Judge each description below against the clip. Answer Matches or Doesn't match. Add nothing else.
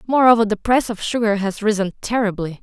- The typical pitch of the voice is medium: Doesn't match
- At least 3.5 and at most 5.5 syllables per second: Doesn't match